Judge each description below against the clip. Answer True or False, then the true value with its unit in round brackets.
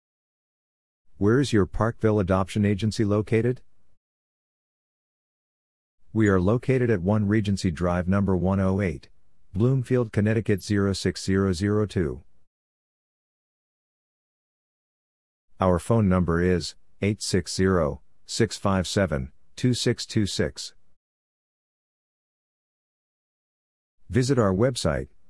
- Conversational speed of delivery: False (65 wpm)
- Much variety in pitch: False (3.4 semitones)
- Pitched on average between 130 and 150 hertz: False (95 Hz)